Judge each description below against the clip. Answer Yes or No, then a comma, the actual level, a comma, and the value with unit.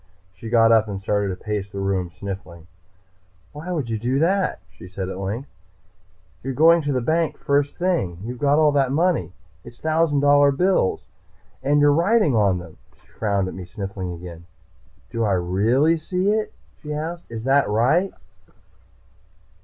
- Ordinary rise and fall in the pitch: No, wide, 7.9 semitones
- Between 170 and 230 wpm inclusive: Yes, average, 175 wpm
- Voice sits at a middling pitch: No, low, 125 Hz